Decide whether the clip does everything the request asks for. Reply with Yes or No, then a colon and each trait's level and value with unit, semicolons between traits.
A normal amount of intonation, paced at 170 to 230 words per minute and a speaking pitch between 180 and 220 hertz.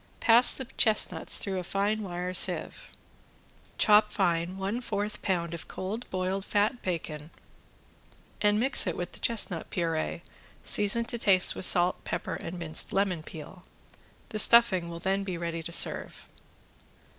No: average, 3.5 semitones; average, 150 wpm; high, 190 Hz